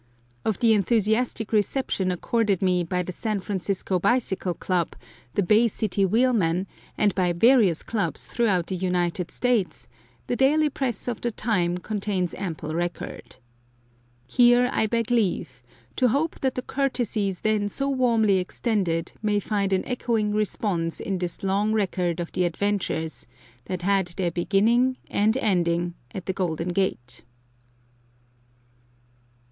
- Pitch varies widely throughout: No, average, 4.2 semitones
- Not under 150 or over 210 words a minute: No, average, 140 wpm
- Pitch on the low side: No, high, 200 Hz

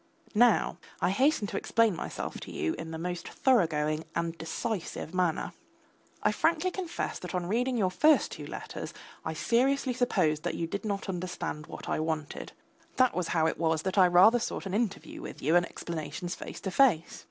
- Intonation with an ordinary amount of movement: No, wide, 6.3 semitones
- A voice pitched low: No, medium, 185 Hz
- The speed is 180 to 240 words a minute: Yes, average, 185 wpm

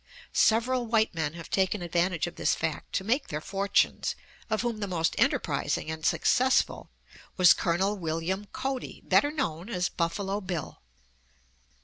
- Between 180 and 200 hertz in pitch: Yes, high, 190 Hz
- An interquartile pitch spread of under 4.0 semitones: No, average, 4.6 semitones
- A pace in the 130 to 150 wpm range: Yes, average, 145 wpm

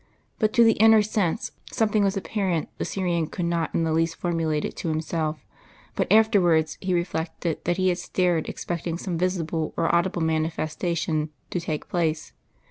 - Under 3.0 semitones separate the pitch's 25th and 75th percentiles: Yes, narrow, 2.6 semitones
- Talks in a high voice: No, medium, 170 Hz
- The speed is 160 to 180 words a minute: Yes, average, 170 wpm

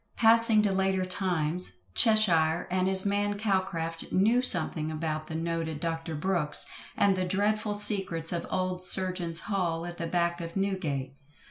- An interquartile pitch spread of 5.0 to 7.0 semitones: No, average, 3.1 semitones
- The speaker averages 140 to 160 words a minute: Yes, average, 150 wpm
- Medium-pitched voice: Yes, medium, 180 Hz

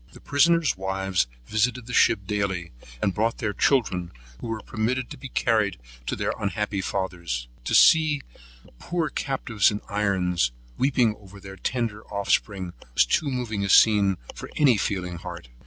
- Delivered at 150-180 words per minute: Yes, average, 160 wpm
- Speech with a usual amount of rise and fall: Yes, average, 4.4 semitones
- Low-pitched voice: Yes, low, 105 Hz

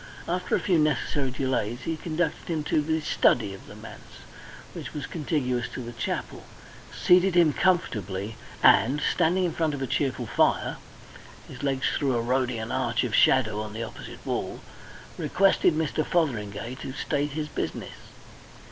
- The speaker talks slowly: No, average, 160 wpm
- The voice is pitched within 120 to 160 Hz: Yes, medium, 140 Hz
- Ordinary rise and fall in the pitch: Yes, average, 5.0 semitones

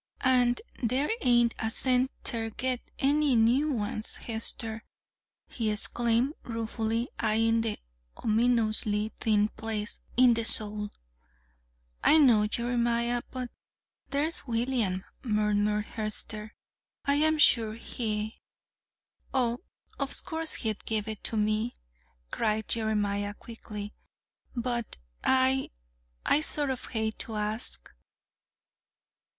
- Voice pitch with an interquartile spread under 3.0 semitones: Yes, narrow, 2.6 semitones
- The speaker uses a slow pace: Yes, slow, 110 wpm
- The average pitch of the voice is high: Yes, high, 230 Hz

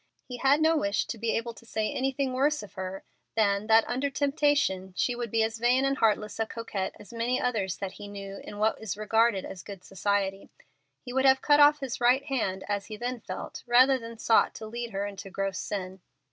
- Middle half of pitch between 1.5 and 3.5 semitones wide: No, average, 4.1 semitones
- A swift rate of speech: Yes, fast, 225 wpm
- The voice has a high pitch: Yes, high, 225 Hz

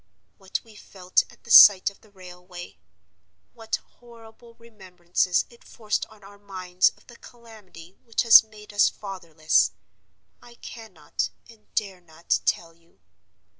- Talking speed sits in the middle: No, slow, 130 wpm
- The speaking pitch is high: Yes, high, 195 Hz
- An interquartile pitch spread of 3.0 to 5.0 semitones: Yes, average, 3.9 semitones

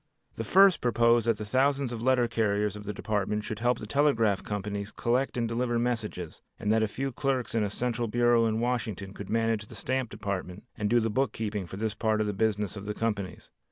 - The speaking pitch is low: Yes, low, 110 Hz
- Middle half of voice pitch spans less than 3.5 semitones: Yes, narrow, 2.6 semitones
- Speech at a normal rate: No, fast, 225 wpm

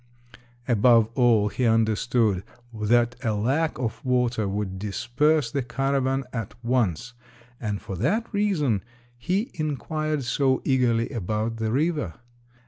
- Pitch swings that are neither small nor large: Yes, average, 3.8 semitones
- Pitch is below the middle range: Yes, low, 120 Hz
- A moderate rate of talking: No, slow, 125 wpm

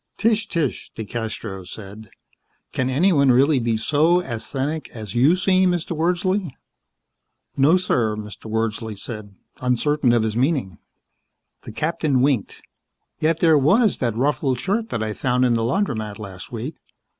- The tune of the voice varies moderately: No, wide, 6.4 semitones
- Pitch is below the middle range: Yes, low, 130 Hz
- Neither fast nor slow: Yes, average, 145 wpm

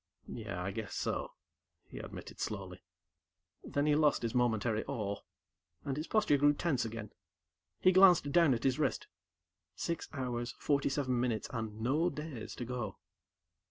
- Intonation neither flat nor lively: Yes, average, 4.6 semitones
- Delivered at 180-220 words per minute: No, average, 155 wpm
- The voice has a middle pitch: No, low, 125 Hz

